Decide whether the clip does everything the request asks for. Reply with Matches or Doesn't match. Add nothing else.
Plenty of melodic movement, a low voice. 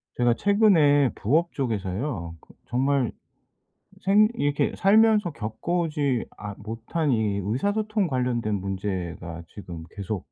Matches